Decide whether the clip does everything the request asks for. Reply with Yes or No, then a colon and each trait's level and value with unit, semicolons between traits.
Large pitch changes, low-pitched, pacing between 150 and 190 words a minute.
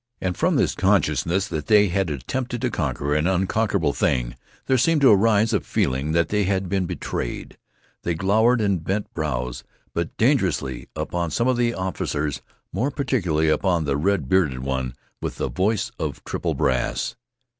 Yes: wide, 5.7 semitones; very low, 95 Hz; average, 165 wpm